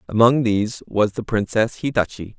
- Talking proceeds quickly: No, average, 150 wpm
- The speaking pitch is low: Yes, low, 110 Hz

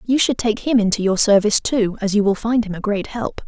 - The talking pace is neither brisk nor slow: No, fast, 275 wpm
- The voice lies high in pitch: Yes, high, 215 Hz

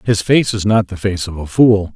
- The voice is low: Yes, low, 100 Hz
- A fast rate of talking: Yes, fast, 275 wpm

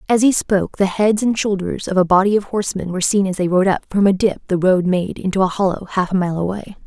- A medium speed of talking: No, fast, 270 wpm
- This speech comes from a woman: Yes, female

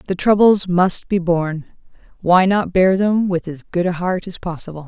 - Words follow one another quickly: No, average, 185 wpm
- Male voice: No, female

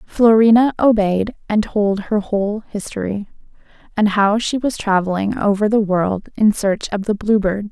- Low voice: No, high, 205 Hz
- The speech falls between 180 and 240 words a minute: No, average, 165 wpm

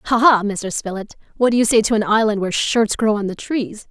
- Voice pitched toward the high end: Yes, high, 215 Hz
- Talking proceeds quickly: Yes, fast, 260 wpm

